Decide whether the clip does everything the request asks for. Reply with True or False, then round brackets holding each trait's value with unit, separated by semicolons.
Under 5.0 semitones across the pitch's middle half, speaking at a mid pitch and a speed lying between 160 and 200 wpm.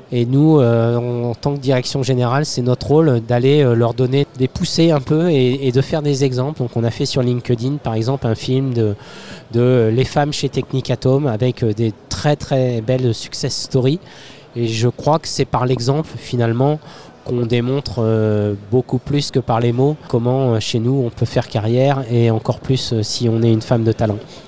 False (2.9 semitones; 130 Hz; 195 wpm)